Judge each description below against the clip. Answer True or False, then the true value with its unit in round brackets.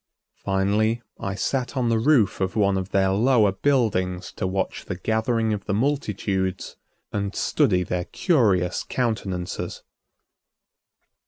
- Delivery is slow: True (130 wpm)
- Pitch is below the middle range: True (100 Hz)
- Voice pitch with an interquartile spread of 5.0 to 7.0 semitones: False (3.4 semitones)